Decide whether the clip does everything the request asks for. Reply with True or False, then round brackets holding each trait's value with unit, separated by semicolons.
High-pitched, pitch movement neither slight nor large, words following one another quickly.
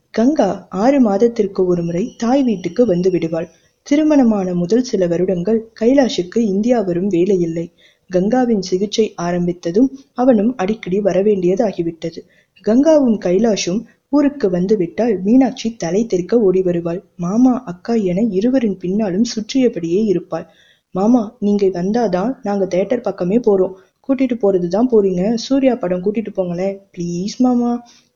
False (205 Hz; 4.5 semitones; 120 wpm)